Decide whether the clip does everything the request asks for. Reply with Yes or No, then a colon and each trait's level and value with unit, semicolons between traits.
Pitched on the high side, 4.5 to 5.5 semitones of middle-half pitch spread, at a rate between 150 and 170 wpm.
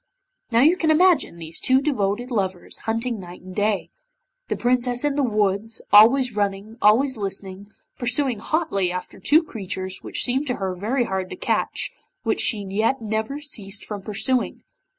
Yes: high, 220 Hz; average, 4.8 semitones; average, 165 wpm